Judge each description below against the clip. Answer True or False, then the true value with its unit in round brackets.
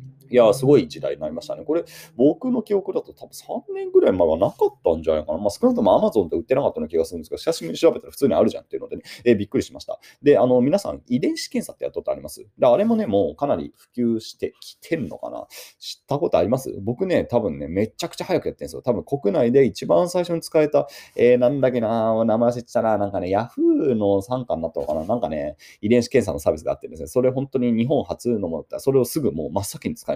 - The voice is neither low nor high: True (145 Hz)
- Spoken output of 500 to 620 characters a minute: True (545 characters per minute)